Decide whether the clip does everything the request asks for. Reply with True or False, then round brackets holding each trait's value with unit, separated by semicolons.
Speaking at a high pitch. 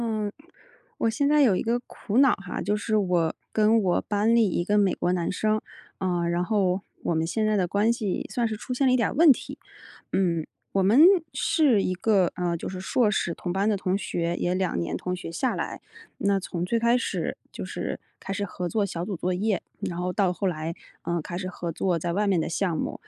True (195 Hz)